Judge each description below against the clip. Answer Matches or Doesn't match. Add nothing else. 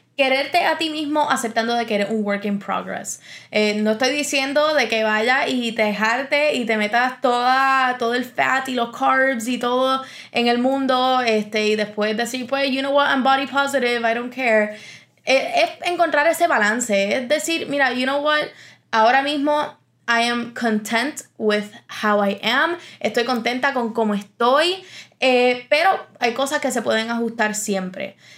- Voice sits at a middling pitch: Doesn't match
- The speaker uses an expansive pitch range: Doesn't match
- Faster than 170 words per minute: Matches